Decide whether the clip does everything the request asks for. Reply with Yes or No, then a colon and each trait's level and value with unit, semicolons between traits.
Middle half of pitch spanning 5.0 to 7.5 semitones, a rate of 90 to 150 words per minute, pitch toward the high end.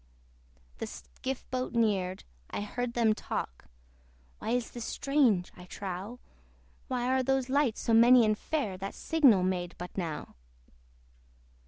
Yes: wide, 5.4 semitones; average, 140 wpm; high, 225 Hz